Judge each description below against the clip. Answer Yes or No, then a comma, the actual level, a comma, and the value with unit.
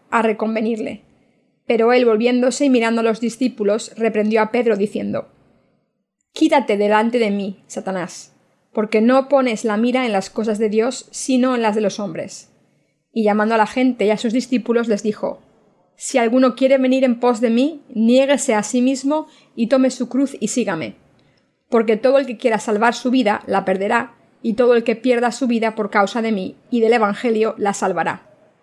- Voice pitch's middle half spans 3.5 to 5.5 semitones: No, average, 2.9 semitones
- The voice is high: Yes, high, 230 Hz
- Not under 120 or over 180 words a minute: No, fast, 190 wpm